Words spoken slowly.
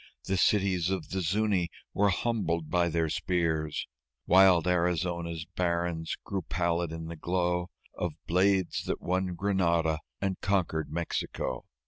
Yes: slow, 130 wpm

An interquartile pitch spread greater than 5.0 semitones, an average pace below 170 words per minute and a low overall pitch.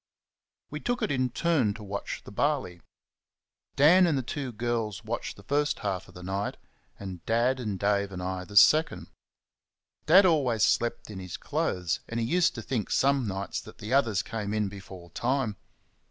No: wide, 5.5 semitones; average, 180 wpm; low, 115 Hz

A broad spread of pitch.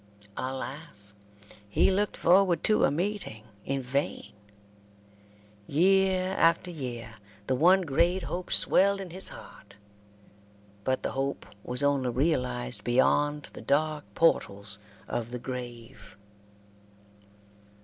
Yes: wide, 6.2 semitones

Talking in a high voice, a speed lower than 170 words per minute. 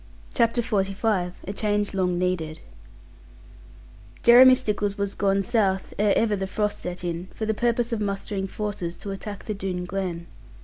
Yes: high, 200 Hz; average, 160 wpm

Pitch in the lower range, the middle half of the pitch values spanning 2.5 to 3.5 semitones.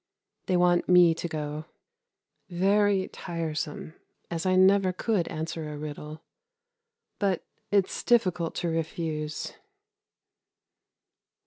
No: medium, 170 Hz; average, 3.0 semitones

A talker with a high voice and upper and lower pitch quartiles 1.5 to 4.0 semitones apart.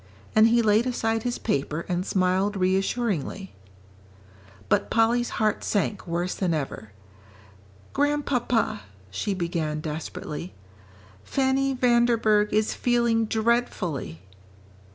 No: high, 210 Hz; average, 5.0 semitones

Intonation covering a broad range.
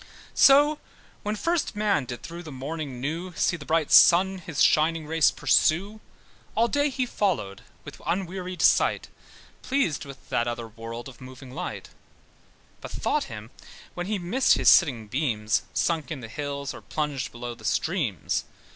Yes: wide, 6.7 semitones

